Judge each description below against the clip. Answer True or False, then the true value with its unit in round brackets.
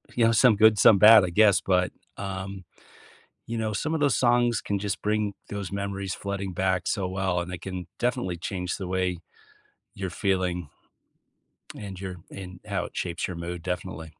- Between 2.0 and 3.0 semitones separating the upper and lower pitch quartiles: True (2.4 semitones)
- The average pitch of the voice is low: True (95 Hz)